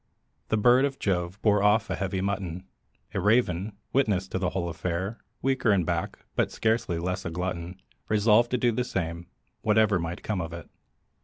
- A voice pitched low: Yes, very low, 95 Hz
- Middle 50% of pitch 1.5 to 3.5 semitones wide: No, average, 3.9 semitones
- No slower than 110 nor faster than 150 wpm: No, average, 180 wpm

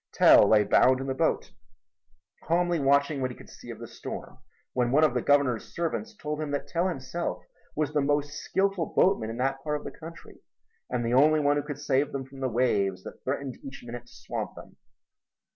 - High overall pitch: No, medium, 140 Hz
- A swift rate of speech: Yes, fast, 210 wpm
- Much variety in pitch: No, average, 3.2 semitones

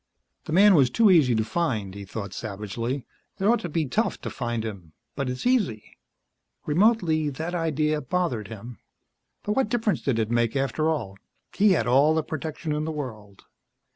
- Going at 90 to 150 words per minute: No, average, 180 wpm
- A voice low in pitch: No, medium, 145 Hz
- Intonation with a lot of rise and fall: Yes, wide, 7.0 semitones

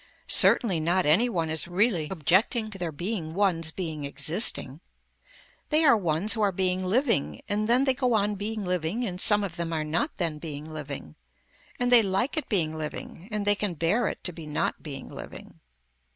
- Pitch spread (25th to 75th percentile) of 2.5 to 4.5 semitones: No, average, 5.0 semitones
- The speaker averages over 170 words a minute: Yes, average, 195 wpm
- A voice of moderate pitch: Yes, medium, 180 Hz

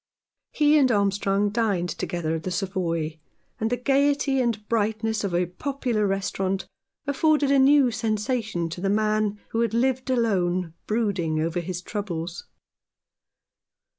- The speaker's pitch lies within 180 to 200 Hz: No, high, 210 Hz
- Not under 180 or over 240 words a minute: No, slow, 135 wpm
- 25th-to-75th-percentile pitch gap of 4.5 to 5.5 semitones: Yes, average, 5.1 semitones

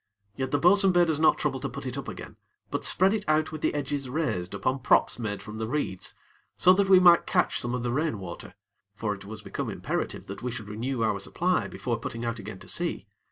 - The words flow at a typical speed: No, fast, 235 wpm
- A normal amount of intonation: No, wide, 6.3 semitones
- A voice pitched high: No, low, 130 Hz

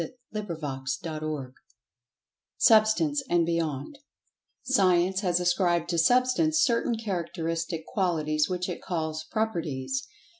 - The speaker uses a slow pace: Yes, slow, 110 wpm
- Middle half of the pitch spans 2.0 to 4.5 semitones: No, wide, 5.5 semitones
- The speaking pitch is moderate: Yes, medium, 175 Hz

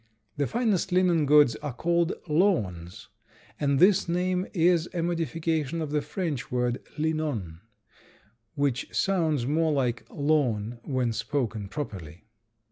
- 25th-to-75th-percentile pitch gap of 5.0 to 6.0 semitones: Yes, wide, 5.6 semitones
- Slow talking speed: Yes, slow, 125 wpm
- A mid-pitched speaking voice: Yes, medium, 150 Hz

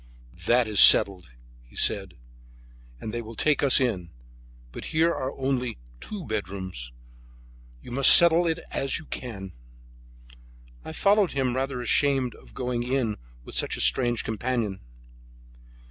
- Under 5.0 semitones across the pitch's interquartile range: Yes, average, 4.1 semitones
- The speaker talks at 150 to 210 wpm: No, average, 140 wpm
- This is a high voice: No, low, 125 Hz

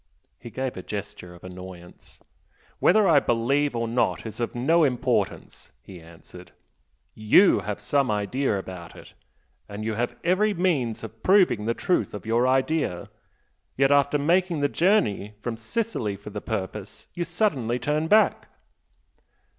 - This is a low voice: Yes, low, 120 Hz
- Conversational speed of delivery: Yes, average, 150 wpm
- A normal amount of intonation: No, wide, 6.4 semitones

